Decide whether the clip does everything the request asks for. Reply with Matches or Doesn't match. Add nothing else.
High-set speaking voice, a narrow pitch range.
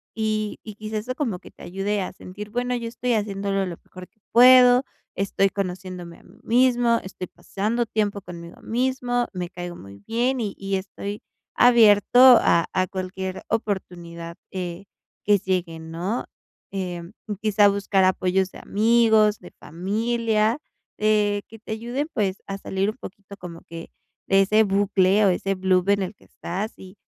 Doesn't match